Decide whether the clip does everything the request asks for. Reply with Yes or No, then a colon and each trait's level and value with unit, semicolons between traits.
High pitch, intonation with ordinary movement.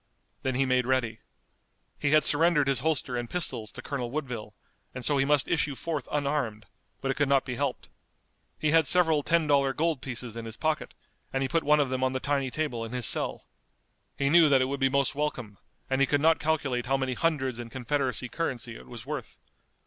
No: low, 135 Hz; average, 3.0 semitones